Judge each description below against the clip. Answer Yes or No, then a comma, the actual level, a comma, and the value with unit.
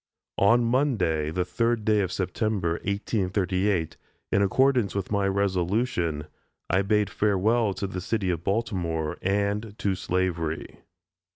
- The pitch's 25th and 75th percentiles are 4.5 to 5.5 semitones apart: No, average, 2.9 semitones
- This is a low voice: Yes, low, 100 Hz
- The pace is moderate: No, slow, 125 wpm